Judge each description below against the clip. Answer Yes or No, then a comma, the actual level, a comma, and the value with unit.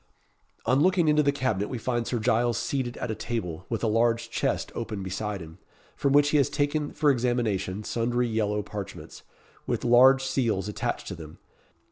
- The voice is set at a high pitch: No, low, 120 Hz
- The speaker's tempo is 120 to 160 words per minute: No, average, 180 wpm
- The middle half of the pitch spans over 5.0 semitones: No, average, 4.1 semitones